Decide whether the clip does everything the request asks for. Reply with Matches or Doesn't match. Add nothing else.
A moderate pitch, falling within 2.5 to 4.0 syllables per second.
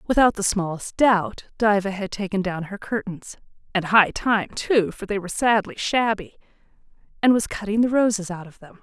Doesn't match